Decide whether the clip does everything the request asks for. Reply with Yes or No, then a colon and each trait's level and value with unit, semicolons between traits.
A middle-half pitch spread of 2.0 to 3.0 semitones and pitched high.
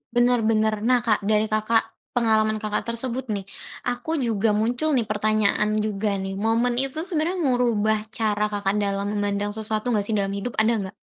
Yes: narrow, 2.6 semitones; high, 220 Hz